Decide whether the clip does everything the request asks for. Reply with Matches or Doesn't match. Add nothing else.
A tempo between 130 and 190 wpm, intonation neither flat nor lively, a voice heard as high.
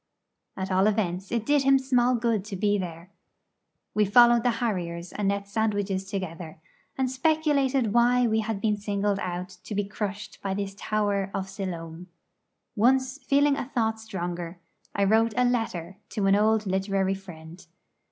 Matches